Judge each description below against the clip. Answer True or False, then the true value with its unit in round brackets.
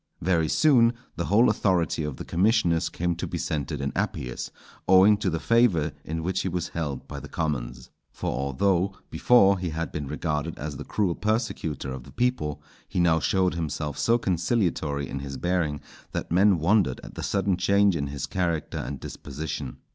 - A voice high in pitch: False (85 Hz)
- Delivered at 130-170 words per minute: False (185 wpm)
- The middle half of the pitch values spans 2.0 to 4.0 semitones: False (4.7 semitones)